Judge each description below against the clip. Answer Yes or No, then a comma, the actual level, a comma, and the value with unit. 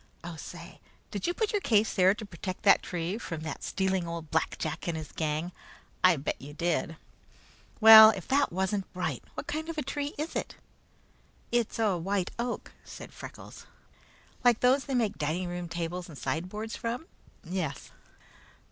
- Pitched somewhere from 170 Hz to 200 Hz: Yes, medium, 185 Hz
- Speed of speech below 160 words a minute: No, average, 170 wpm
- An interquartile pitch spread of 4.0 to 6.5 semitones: Yes, wide, 5.4 semitones